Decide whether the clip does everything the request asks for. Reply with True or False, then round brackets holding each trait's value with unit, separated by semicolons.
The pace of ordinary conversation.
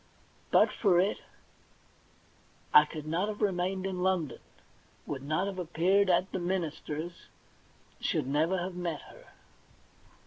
False (130 wpm)